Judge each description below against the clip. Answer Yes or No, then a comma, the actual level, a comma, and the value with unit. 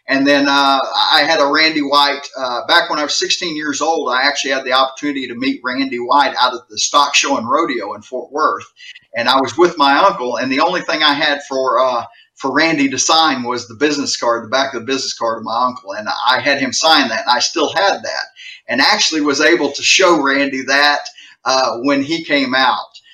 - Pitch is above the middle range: No, medium, 140 Hz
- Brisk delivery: Yes, fast, 235 wpm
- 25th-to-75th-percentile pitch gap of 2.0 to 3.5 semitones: Yes, average, 3.2 semitones